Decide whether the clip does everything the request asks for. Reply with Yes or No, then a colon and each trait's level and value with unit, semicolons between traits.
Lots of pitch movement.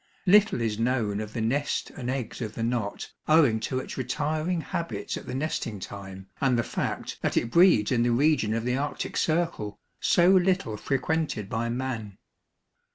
Yes: wide, 5.7 semitones